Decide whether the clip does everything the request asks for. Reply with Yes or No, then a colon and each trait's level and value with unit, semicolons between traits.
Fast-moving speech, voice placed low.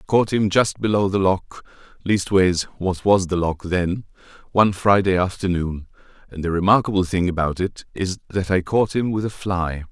No: average, 170 wpm; very low, 95 Hz